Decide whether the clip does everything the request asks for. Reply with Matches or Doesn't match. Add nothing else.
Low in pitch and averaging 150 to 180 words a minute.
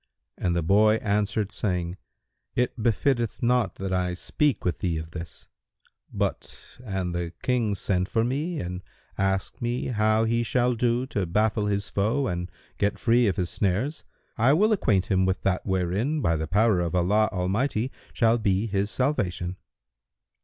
Matches